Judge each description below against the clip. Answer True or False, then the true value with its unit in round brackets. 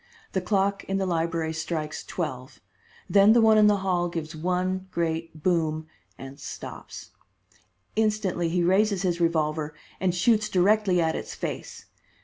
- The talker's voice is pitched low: False (175 Hz)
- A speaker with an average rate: True (145 wpm)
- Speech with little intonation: False (3.4 semitones)